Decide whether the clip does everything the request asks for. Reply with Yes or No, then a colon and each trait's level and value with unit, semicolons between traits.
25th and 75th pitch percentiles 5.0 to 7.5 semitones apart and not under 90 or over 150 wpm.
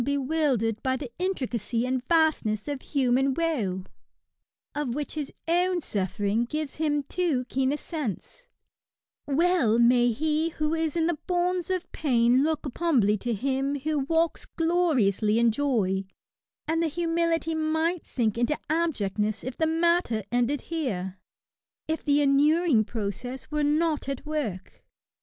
Yes: average, 5.3 semitones; average, 145 wpm